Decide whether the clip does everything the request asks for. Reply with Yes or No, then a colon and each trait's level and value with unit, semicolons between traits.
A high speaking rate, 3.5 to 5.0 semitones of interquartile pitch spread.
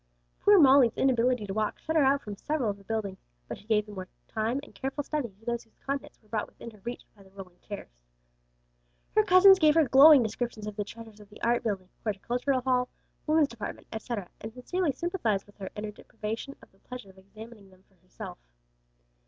Yes: fast, 215 wpm; average, 4.7 semitones